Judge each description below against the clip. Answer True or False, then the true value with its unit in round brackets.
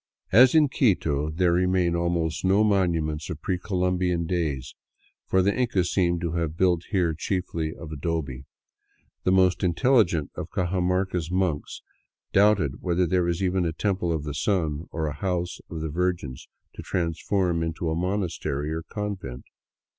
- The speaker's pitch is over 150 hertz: False (85 Hz)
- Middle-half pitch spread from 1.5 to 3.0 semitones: True (2.6 semitones)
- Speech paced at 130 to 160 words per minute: True (155 wpm)